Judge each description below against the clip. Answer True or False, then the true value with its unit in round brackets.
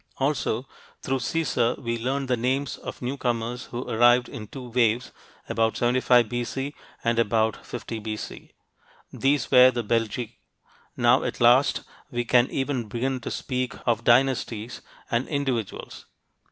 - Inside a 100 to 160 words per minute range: True (140 wpm)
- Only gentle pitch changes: True (2.0 semitones)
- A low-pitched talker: True (120 Hz)